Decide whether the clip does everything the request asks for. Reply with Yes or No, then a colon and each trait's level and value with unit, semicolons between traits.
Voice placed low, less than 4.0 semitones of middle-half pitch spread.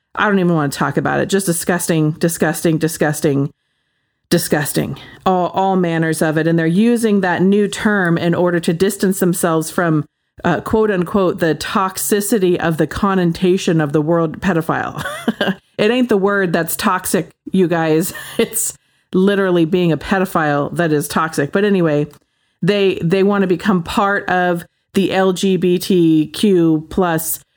No: medium, 180 Hz; average, 3.3 semitones